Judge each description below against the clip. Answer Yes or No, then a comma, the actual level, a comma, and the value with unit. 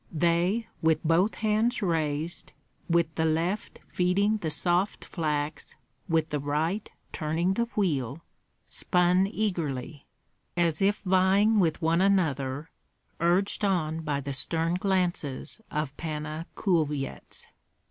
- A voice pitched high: No, medium, 170 Hz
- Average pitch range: Yes, average, 3.8 semitones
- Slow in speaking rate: Yes, slow, 115 wpm